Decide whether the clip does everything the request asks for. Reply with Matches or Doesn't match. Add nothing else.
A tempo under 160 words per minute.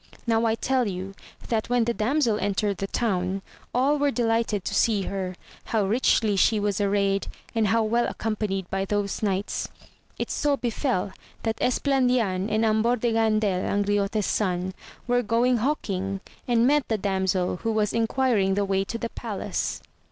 Doesn't match